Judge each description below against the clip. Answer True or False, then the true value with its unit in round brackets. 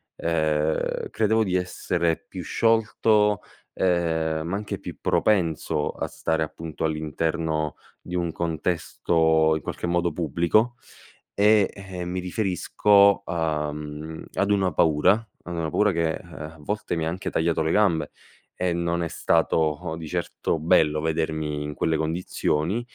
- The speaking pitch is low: True (85 Hz)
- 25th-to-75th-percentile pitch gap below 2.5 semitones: False (2.8 semitones)